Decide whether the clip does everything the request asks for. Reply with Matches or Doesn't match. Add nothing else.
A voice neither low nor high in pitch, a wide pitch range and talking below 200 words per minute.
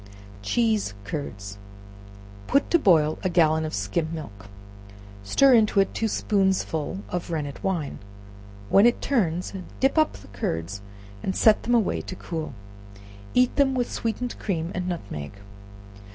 Matches